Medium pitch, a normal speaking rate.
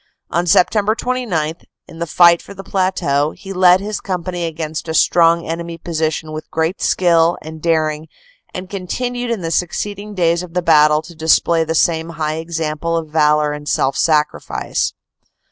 Yes: medium, 165 Hz; average, 165 wpm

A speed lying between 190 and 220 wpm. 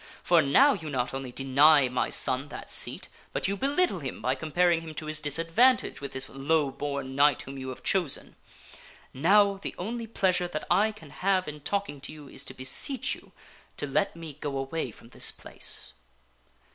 Yes: average, 195 wpm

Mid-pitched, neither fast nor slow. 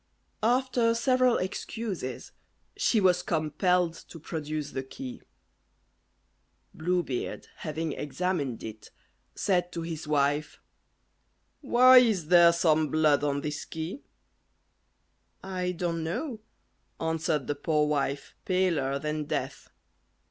No: medium, 165 Hz; slow, 110 wpm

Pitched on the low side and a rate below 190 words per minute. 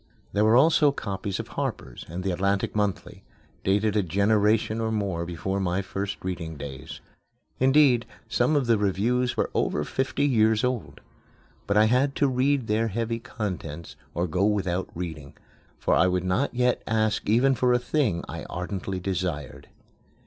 Yes: low, 105 Hz; average, 165 wpm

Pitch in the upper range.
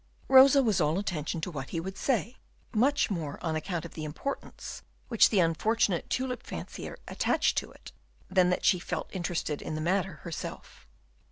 No: medium, 180 Hz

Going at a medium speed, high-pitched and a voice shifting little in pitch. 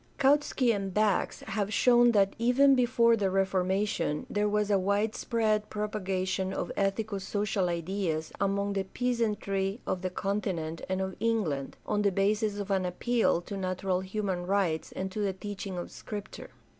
Yes: average, 155 wpm; high, 200 Hz; narrow, 2.1 semitones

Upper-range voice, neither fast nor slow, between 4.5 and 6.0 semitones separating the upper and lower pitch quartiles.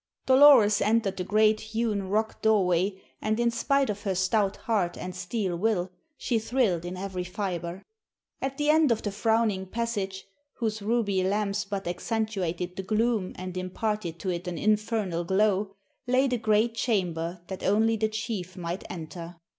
No: high, 205 Hz; average, 160 wpm; average, 3.4 semitones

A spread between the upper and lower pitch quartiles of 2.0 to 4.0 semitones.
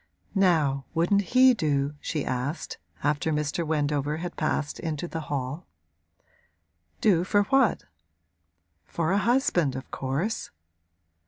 No: average, 4.7 semitones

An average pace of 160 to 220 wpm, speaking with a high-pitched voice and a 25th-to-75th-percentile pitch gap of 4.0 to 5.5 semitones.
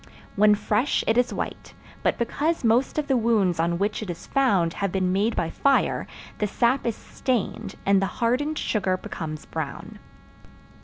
Yes: average, 170 wpm; high, 210 Hz; average, 4.6 semitones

